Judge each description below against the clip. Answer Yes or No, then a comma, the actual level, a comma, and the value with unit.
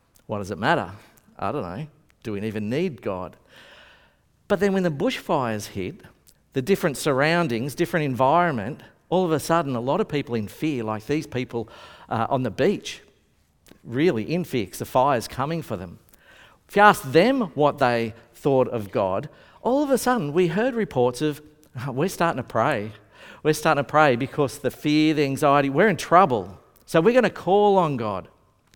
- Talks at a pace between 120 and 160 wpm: No, average, 185 wpm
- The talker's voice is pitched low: No, medium, 145 Hz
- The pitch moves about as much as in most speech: No, wide, 6.6 semitones